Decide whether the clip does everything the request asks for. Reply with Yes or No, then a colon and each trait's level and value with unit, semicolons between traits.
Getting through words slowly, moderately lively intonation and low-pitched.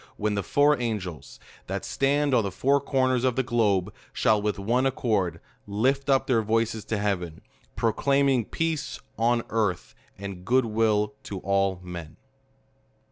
No: average, 150 wpm; average, 4.7 semitones; low, 110 Hz